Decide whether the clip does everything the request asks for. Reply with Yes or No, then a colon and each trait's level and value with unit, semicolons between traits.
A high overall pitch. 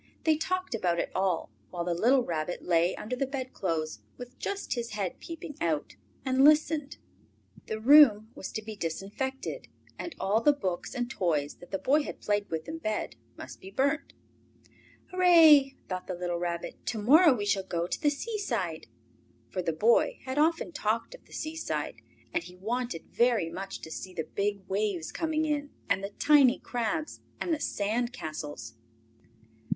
Yes: high, 220 Hz